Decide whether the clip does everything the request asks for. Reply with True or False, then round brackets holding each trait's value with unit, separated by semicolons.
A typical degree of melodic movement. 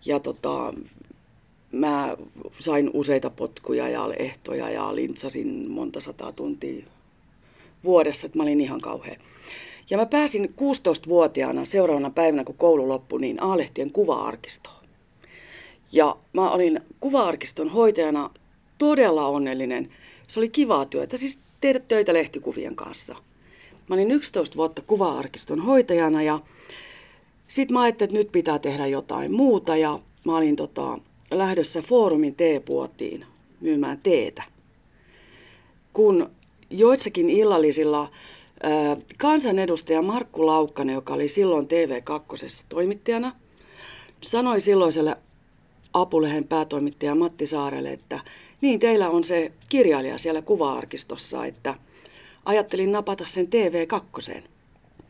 False (8.7 semitones)